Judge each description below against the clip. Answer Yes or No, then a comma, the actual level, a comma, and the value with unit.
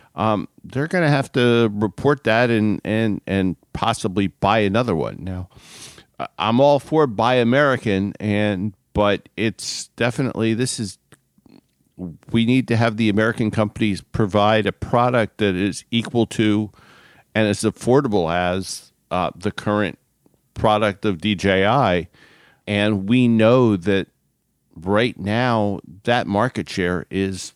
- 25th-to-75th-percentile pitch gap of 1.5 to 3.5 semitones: Yes, average, 2.8 semitones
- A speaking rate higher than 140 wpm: No, slow, 135 wpm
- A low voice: Yes, low, 110 Hz